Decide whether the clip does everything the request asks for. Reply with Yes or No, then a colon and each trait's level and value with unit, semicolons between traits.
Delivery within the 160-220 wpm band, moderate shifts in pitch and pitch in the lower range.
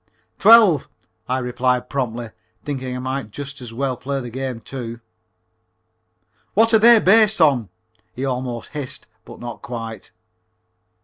No: slow, 135 wpm; average, 3.0 semitones; low, 130 Hz